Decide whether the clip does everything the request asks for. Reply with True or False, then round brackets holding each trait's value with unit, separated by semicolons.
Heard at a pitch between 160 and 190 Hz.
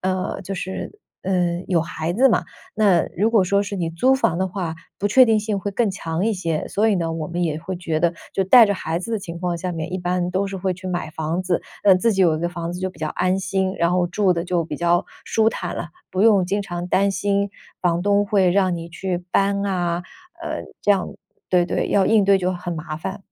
True (185 Hz)